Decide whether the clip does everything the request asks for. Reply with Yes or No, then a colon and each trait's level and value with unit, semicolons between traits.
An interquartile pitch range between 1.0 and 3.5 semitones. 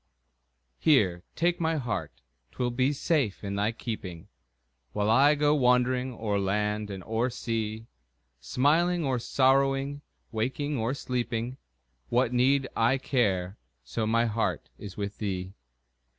No: average, 4.5 semitones